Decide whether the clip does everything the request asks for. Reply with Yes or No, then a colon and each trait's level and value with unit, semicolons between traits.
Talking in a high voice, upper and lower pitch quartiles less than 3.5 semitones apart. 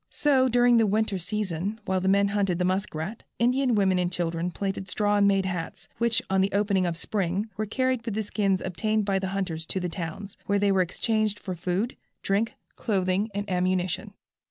Yes: high, 195 Hz; narrow, 2.6 semitones